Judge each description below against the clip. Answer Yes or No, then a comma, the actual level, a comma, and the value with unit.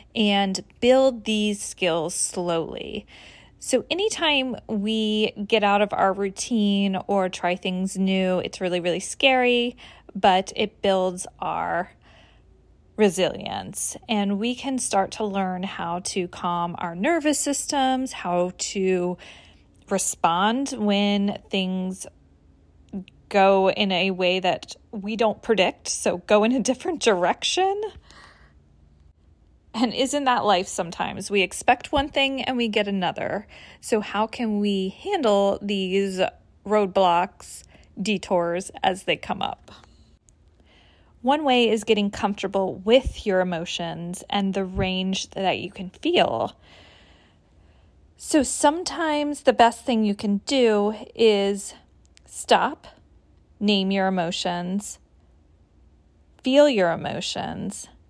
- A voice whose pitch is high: Yes, high, 200 Hz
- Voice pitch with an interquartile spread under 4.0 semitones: No, average, 4.4 semitones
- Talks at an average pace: No, slow, 115 wpm